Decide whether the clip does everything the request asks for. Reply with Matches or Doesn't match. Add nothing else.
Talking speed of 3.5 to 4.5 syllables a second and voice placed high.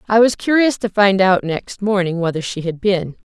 Doesn't match